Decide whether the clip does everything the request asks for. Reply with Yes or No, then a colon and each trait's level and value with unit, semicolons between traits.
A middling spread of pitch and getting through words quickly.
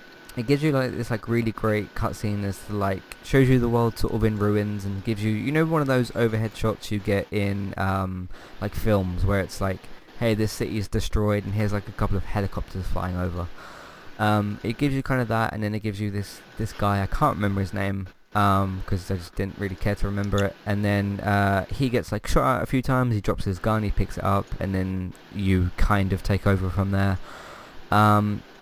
No: narrow, 2.3 semitones; fast, 235 wpm